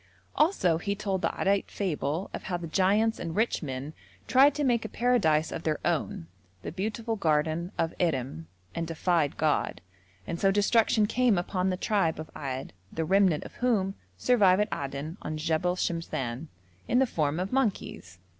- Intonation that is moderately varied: Yes, average, 5.0 semitones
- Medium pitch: Yes, medium, 180 Hz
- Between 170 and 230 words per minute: Yes, average, 175 wpm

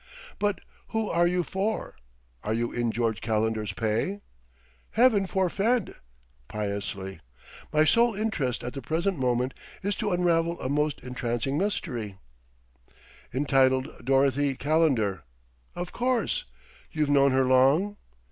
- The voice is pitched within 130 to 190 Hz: Yes, medium, 140 Hz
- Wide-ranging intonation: Yes, wide, 7.8 semitones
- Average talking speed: No, slow, 125 wpm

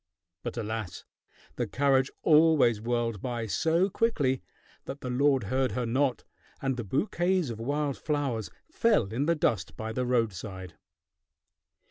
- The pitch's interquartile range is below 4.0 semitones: No, average, 4.3 semitones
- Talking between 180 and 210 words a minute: No, average, 140 wpm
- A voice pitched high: No, low, 125 Hz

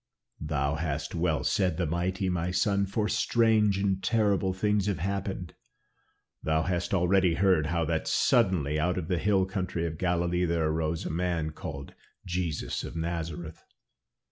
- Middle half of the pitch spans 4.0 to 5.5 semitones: No, average, 2.9 semitones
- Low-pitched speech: Yes, very low, 90 Hz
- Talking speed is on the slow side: No, average, 155 wpm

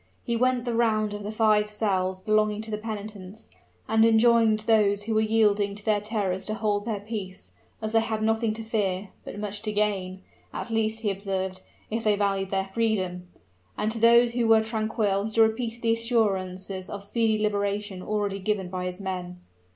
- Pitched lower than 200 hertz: No, high, 210 Hz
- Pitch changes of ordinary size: No, narrow, 2.1 semitones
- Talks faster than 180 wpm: Yes, average, 190 wpm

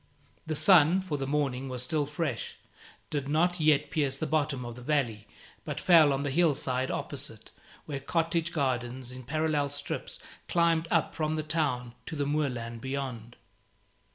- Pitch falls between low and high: Yes, medium, 145 Hz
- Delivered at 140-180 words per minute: Yes, average, 165 wpm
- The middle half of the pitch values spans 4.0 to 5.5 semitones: No, average, 3.3 semitones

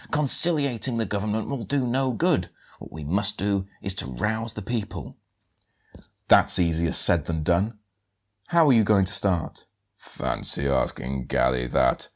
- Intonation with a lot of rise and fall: Yes, wide, 5.7 semitones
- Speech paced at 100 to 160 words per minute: Yes, average, 155 wpm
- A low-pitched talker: Yes, low, 100 Hz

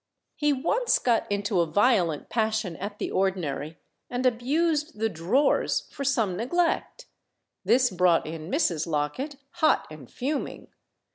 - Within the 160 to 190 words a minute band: No, slow, 135 wpm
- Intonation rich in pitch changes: Yes, wide, 8.3 semitones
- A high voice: Yes, high, 220 Hz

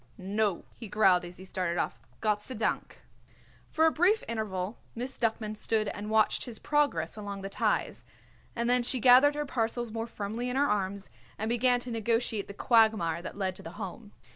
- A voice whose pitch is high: Yes, high, 220 Hz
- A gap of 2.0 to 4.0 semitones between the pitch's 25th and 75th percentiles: Yes, average, 3.3 semitones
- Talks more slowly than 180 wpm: No, average, 190 wpm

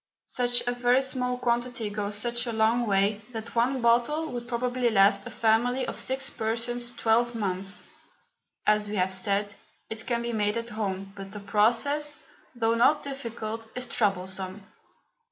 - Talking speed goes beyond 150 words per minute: Yes, average, 160 wpm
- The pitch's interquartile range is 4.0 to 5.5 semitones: No, average, 2.8 semitones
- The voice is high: Yes, high, 230 Hz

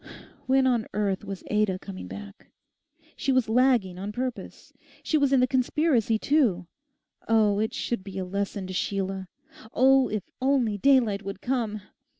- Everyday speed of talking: Yes, average, 160 wpm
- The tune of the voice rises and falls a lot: No, average, 4.6 semitones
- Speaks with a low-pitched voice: No, high, 215 Hz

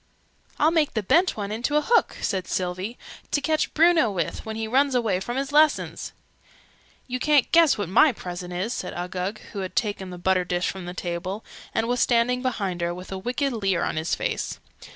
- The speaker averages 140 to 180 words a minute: No, fast, 205 wpm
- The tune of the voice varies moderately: No, wide, 6.1 semitones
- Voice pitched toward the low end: No, high, 215 Hz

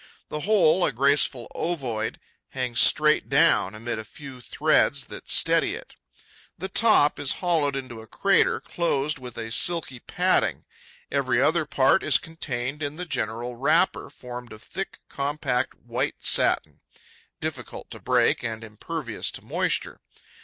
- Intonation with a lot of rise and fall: No, average, 4.4 semitones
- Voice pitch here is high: No, low, 135 Hz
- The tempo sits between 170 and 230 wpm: No, average, 145 wpm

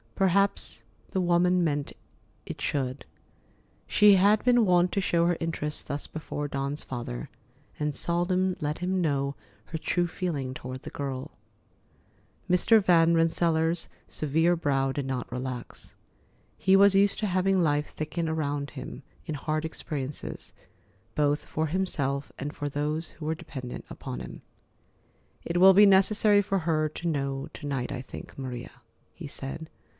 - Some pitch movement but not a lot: Yes, average, 4.3 semitones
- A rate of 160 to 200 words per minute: No, average, 150 wpm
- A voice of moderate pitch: Yes, medium, 160 Hz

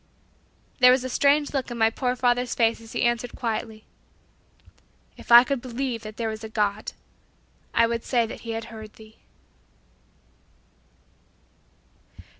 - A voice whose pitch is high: Yes, high, 235 Hz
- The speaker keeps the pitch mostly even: Yes, narrow, 2.0 semitones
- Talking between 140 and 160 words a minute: Yes, average, 150 wpm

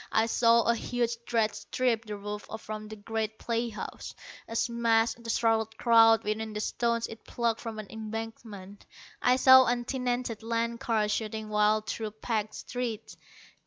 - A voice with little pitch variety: Yes, narrow, 1.5 semitones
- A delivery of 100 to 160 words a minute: Yes, average, 155 wpm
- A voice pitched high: Yes, high, 225 Hz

